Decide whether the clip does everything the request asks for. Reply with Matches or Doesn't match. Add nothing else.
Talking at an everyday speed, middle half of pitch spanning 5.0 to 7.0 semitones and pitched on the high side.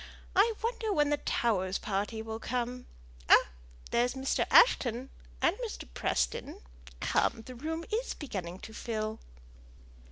Doesn't match